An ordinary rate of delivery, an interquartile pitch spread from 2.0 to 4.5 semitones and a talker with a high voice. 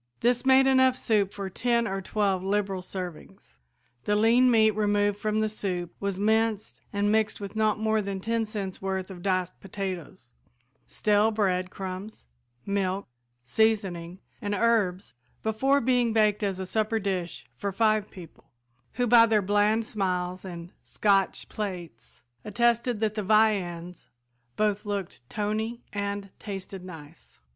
Yes: average, 145 wpm; narrow, 2.6 semitones; high, 205 Hz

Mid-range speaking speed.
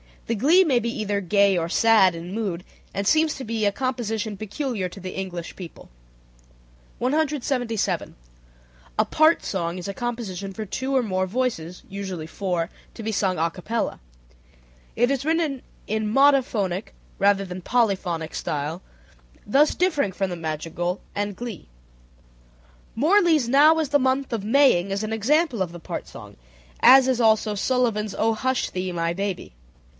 Yes: average, 160 wpm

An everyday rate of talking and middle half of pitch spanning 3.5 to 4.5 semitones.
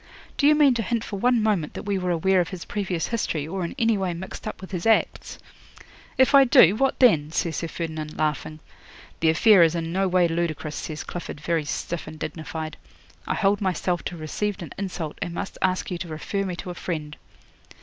No: fast, 220 wpm; average, 4.0 semitones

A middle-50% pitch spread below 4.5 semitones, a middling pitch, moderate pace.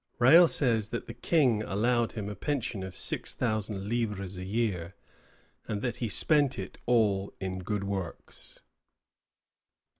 No: average, 3.5 semitones; low, 110 Hz; average, 145 wpm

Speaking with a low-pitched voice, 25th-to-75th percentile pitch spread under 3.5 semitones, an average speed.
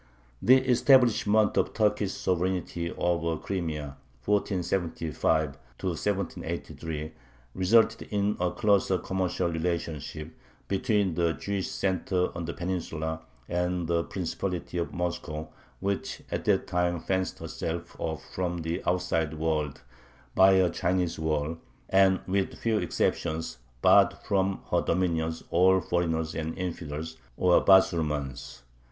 No: very low, 90 Hz; average, 2.8 semitones; slow, 120 wpm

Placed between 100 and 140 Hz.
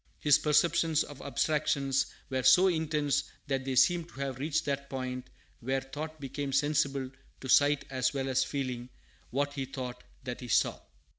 Yes: low, 135 Hz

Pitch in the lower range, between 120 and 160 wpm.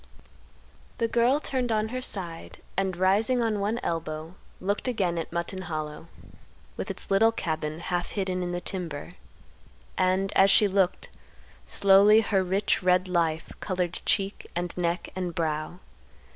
No: medium, 185 Hz; average, 145 wpm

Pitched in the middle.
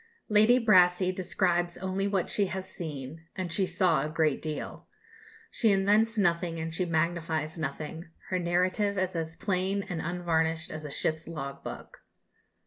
Yes: medium, 175 Hz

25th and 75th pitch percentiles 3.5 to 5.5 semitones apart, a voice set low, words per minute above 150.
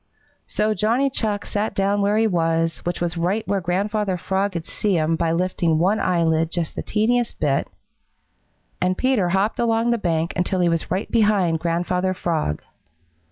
No: average, 3.9 semitones; medium, 185 Hz; average, 170 wpm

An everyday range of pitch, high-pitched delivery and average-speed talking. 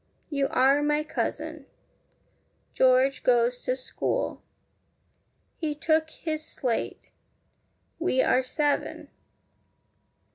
No: average, 3.3 semitones; very high, 280 Hz; slow, 85 wpm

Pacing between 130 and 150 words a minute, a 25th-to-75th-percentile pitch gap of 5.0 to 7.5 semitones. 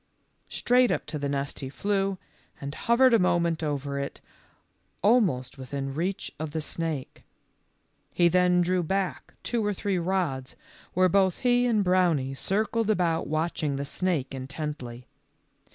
Yes: average, 145 wpm; wide, 5.6 semitones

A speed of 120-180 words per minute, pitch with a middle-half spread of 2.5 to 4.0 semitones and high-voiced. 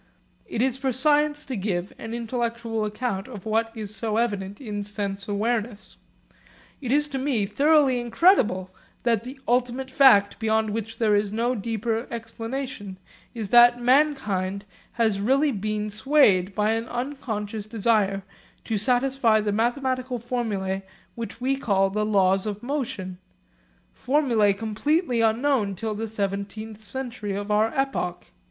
Yes: average, 140 wpm; average, 3.6 semitones; high, 225 Hz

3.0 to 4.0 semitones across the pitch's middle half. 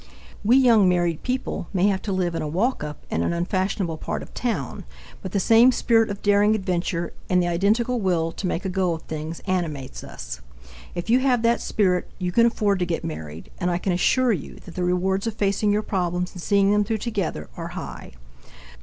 Yes: average, 3.6 semitones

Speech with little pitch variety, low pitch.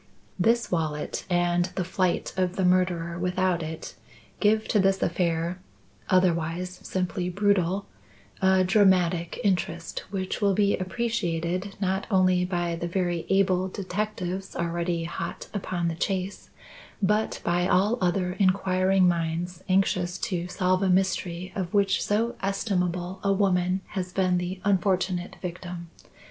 No: narrow, 1.7 semitones; medium, 185 Hz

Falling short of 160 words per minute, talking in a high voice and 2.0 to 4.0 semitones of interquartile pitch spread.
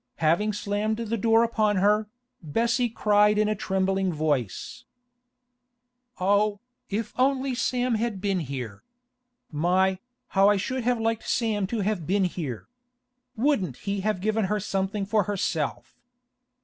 Yes: slow, 135 wpm; high, 205 Hz; average, 2.9 semitones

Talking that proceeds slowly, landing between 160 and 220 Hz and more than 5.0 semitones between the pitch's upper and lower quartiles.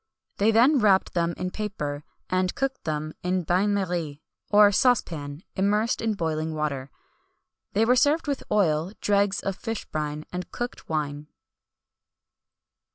No: average, 145 wpm; medium, 185 Hz; wide, 5.4 semitones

